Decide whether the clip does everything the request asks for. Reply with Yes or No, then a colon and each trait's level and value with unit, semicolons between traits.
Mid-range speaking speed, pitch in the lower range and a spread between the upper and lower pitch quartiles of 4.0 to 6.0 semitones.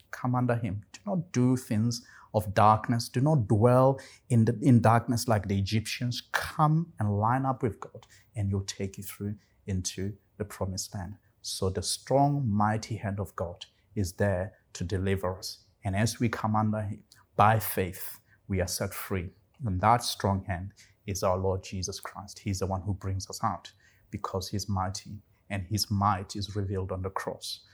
No: average, 185 wpm; low, 105 Hz; average, 2.8 semitones